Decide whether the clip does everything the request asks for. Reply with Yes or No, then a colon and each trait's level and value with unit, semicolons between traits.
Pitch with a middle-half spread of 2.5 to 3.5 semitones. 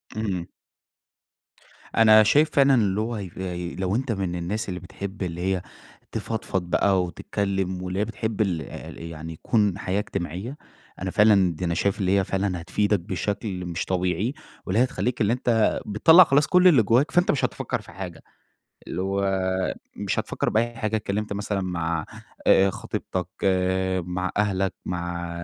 Yes: average, 3.1 semitones